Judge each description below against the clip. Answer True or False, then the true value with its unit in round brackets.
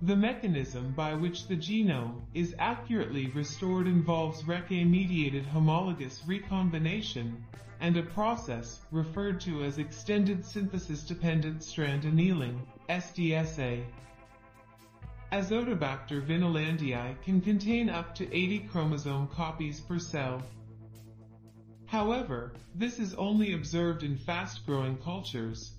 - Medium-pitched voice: True (160 Hz)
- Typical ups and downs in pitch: False (6.0 semitones)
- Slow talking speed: True (100 wpm)